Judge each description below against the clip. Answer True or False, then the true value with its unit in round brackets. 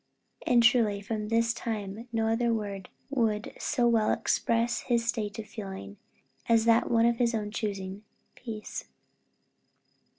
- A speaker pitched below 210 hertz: False (225 Hz)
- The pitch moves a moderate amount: False (1.9 semitones)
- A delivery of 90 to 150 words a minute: True (140 wpm)